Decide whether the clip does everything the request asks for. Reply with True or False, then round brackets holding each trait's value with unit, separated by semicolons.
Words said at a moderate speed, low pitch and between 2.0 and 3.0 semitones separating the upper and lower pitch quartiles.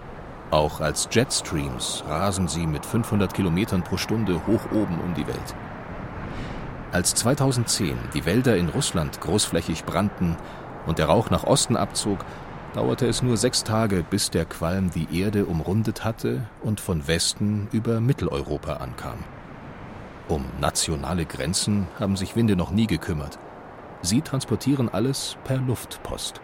False (140 wpm; 105 Hz; 4.5 semitones)